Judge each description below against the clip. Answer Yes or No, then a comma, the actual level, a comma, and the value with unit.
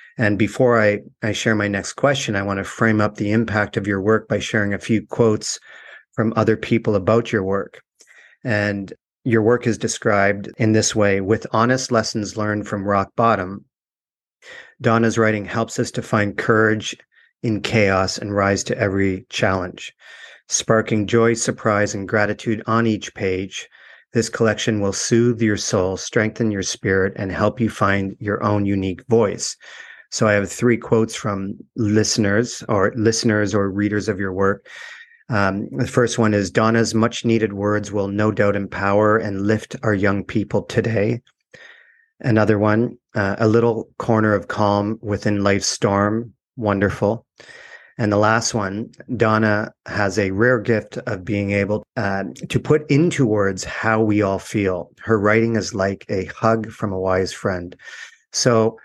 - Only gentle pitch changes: Yes, narrow, 2.1 semitones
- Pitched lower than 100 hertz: No, low, 110 Hz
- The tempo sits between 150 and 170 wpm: Yes, average, 165 wpm